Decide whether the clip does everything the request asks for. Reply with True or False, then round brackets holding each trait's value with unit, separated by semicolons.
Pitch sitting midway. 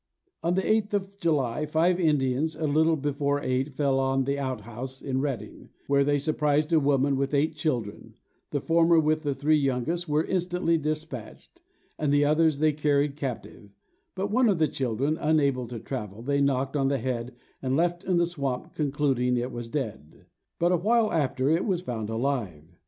True (145 Hz)